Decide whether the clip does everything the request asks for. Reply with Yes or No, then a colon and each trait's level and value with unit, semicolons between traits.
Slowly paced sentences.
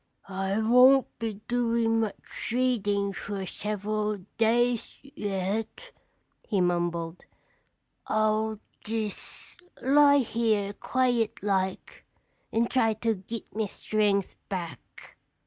Yes: slow, 95 wpm